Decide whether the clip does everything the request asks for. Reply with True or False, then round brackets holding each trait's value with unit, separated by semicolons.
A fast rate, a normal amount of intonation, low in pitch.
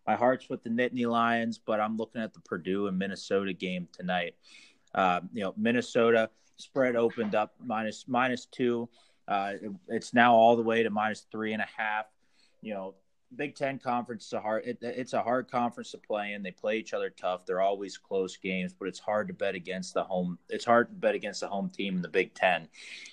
True (215 wpm; 3.7 semitones; 110 Hz)